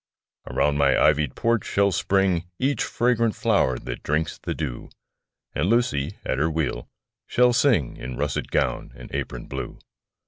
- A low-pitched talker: Yes, very low, 80 Hz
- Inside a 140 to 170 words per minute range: Yes, average, 150 wpm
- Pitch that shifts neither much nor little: No, wide, 8.4 semitones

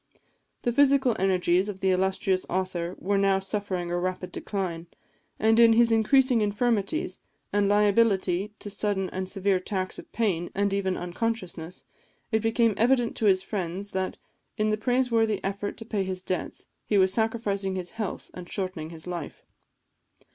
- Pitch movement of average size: Yes, average, 3.1 semitones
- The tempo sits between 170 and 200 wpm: No, average, 160 wpm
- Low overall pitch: No, high, 200 Hz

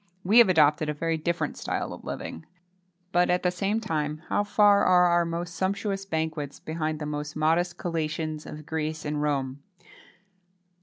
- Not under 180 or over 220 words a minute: No, average, 165 wpm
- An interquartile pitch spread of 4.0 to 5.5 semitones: No, average, 2.8 semitones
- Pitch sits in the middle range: Yes, medium, 160 Hz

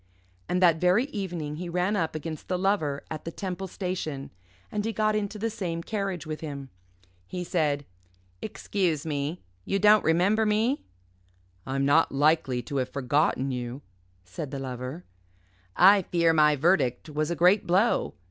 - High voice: No, medium, 165 Hz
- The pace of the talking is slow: No, average, 160 wpm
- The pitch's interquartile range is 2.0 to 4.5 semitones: No, average, 5.1 semitones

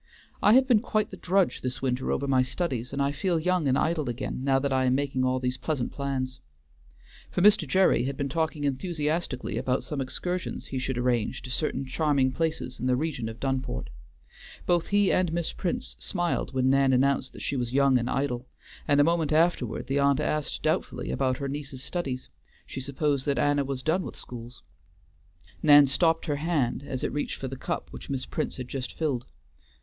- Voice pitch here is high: No, medium, 140 Hz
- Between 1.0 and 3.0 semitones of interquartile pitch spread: No, average, 3.5 semitones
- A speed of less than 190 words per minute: No, average, 200 wpm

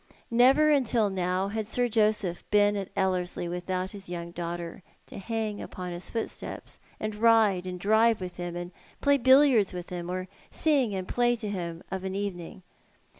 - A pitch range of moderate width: Yes, average, 3.9 semitones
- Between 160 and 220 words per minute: Yes, average, 175 wpm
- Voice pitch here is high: Yes, high, 195 Hz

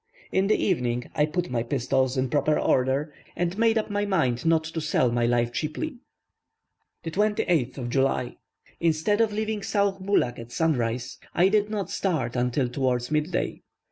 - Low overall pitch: No, medium, 155 Hz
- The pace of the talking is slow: No, average, 165 wpm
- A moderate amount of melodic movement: No, wide, 7.6 semitones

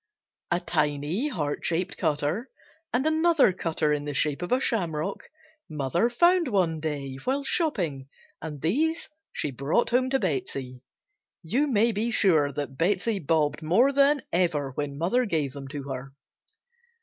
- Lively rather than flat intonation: Yes, wide, 8.5 semitones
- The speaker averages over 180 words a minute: No, average, 150 wpm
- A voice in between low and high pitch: Yes, medium, 165 Hz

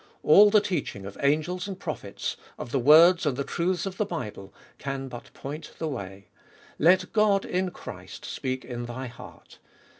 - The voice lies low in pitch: No, medium, 150 Hz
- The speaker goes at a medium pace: Yes, average, 175 wpm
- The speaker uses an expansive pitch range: Yes, wide, 6.5 semitones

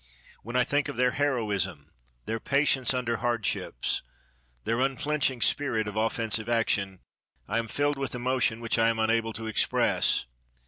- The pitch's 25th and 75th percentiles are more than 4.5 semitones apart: No, average, 2.9 semitones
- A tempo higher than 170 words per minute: No, average, 150 wpm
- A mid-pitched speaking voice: No, low, 115 Hz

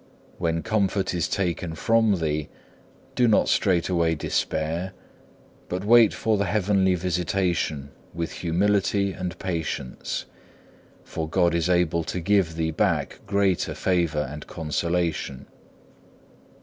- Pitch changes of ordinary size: Yes, average, 3.1 semitones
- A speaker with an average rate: No, slow, 115 wpm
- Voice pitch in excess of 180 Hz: No, very low, 90 Hz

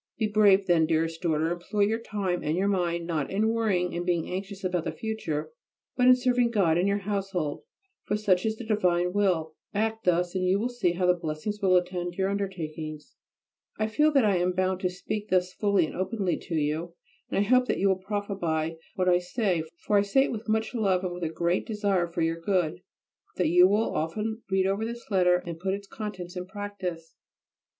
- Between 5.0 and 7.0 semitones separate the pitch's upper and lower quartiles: No, average, 3.1 semitones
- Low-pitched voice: No, medium, 185 Hz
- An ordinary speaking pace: No, fast, 215 wpm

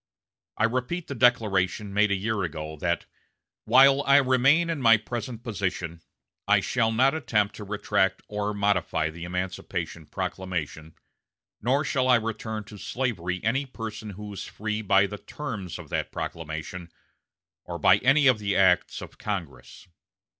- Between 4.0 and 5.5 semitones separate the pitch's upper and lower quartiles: Yes, average, 4.9 semitones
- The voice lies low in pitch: Yes, low, 105 Hz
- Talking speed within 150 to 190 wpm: Yes, average, 155 wpm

